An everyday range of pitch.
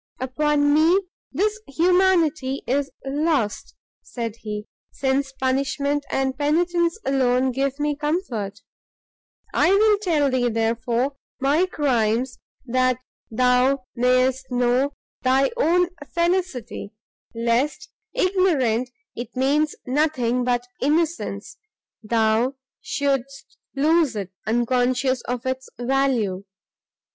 Yes: average, 3.6 semitones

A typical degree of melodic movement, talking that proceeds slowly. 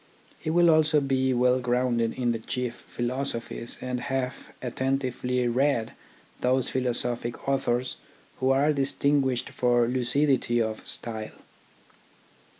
No: narrow, 1.9 semitones; slow, 120 wpm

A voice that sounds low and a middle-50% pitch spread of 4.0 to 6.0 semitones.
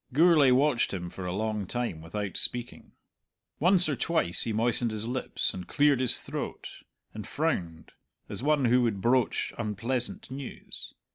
Yes: low, 120 Hz; average, 4.7 semitones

